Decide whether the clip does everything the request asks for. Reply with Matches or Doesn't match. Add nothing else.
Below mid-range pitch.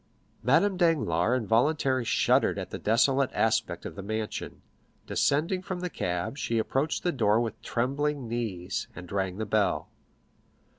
Matches